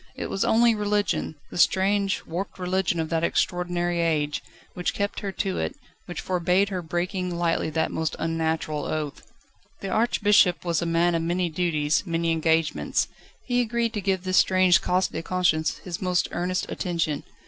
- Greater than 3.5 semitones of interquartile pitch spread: No, narrow, 2.6 semitones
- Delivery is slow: No, average, 170 wpm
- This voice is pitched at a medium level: Yes, medium, 175 Hz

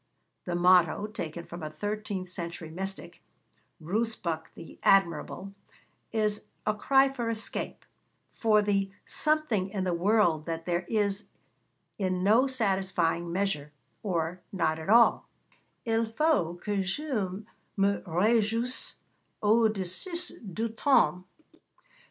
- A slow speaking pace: Yes, slow, 115 wpm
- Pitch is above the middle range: Yes, high, 195 Hz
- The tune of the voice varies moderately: Yes, average, 4.1 semitones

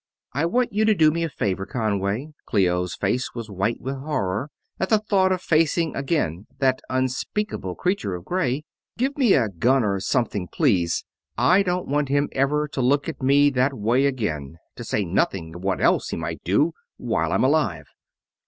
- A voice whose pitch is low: Yes, low, 130 Hz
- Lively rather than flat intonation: Yes, wide, 8.0 semitones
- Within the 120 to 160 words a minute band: No, average, 185 wpm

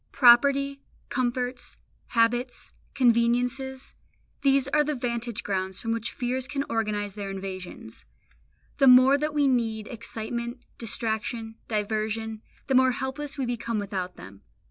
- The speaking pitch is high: Yes, high, 240 Hz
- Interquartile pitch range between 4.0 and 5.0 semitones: No, average, 3.1 semitones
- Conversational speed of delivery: No, slow, 125 wpm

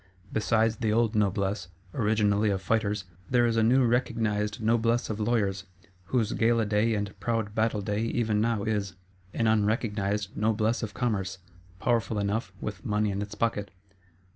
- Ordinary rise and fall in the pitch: No, narrow, 1.9 semitones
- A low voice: Yes, low, 110 Hz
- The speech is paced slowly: No, average, 155 wpm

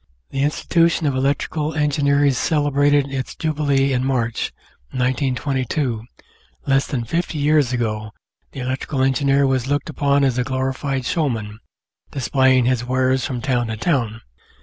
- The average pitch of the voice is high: No, low, 135 Hz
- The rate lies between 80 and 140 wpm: Yes, slow, 135 wpm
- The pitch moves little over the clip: Yes, narrow, 2.3 semitones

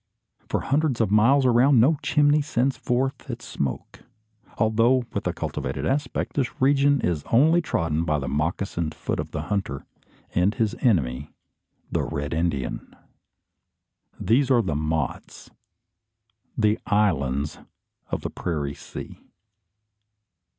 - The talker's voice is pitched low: Yes, low, 105 Hz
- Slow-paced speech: Yes, slow, 130 wpm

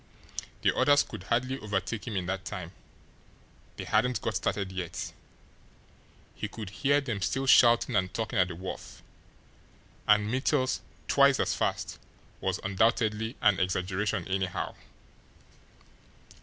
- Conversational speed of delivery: No, slow, 130 wpm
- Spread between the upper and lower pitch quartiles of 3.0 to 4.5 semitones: No, average, 4.9 semitones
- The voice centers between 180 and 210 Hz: No, low, 105 Hz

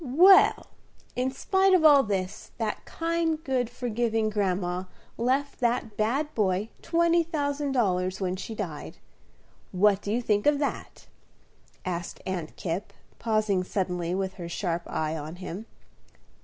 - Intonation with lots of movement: Yes, wide, 6.8 semitones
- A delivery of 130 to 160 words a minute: Yes, average, 140 wpm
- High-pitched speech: Yes, high, 215 Hz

